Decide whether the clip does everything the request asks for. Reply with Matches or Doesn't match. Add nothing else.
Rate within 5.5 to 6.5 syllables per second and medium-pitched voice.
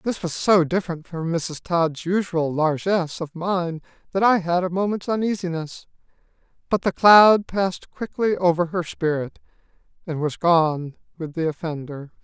Doesn't match